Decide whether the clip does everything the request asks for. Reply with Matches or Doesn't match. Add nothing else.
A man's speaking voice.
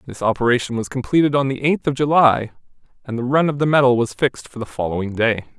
Matches